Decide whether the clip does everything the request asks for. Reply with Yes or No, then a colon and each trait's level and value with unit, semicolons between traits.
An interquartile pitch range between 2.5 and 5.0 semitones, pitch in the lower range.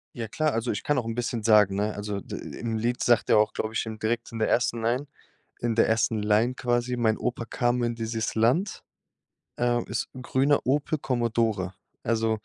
No: narrow, 1.8 semitones; low, 115 Hz